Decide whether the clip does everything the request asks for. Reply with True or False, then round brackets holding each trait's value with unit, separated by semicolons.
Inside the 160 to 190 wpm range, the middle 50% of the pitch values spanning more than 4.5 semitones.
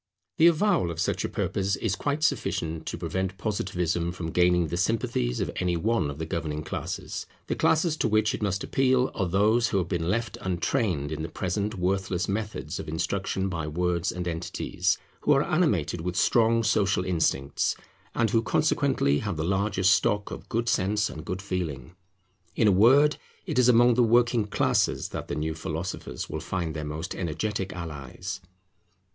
True (180 wpm; 5.0 semitones)